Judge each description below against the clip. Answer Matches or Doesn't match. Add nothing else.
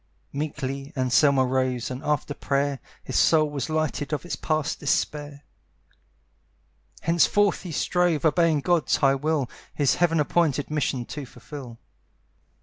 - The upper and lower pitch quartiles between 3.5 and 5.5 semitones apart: Doesn't match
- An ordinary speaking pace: Doesn't match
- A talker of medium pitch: Matches